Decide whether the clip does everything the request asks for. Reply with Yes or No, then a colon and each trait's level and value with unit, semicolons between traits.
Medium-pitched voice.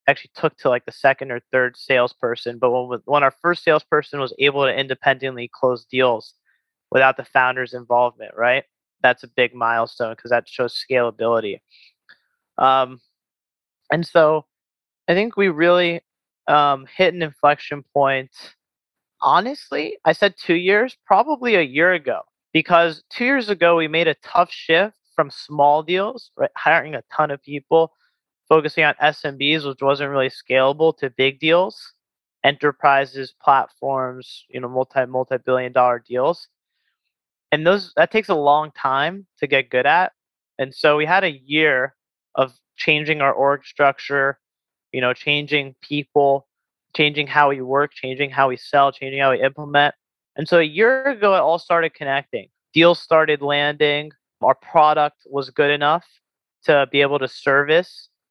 Yes: medium, 145 Hz